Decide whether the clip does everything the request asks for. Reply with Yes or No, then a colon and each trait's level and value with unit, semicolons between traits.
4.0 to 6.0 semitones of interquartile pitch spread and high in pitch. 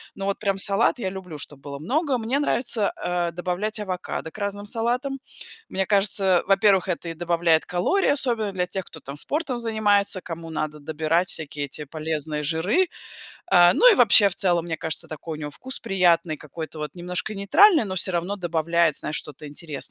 No: average, 4.5 semitones; medium, 180 Hz